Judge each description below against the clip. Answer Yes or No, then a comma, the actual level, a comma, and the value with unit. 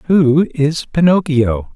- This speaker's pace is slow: Yes, slow, 105 wpm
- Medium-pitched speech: Yes, medium, 150 Hz